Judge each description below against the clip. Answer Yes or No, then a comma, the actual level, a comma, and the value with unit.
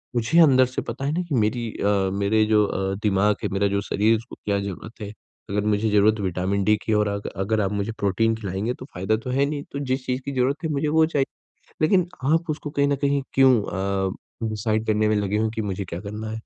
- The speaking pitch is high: No, low, 110 Hz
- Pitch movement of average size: Yes, average, 4.5 semitones